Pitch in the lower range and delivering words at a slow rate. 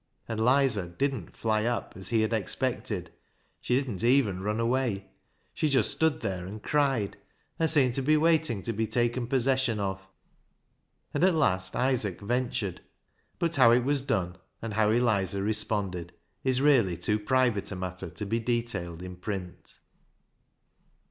No: low, 115 Hz; average, 155 wpm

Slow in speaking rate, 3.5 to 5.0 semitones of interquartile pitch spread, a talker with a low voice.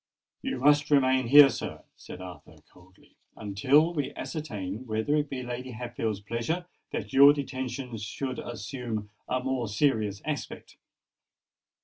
Yes: slow, 130 wpm; average, 4.4 semitones; low, 125 Hz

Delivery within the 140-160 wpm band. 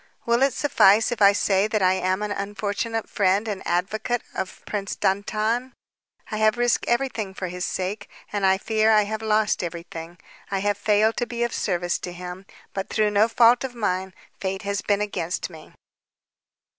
No: average, 180 wpm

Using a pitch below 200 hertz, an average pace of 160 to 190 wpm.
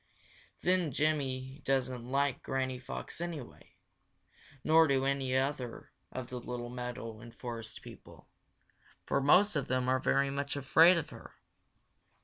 No: low, 135 Hz; slow, 135 wpm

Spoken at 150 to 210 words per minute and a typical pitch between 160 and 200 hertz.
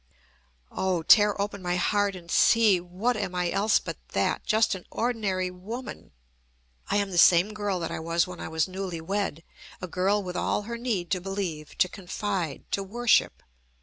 Yes: average, 180 wpm; high, 190 Hz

